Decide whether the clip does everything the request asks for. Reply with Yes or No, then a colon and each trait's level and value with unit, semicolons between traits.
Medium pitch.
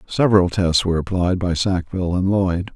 No: very low, 90 Hz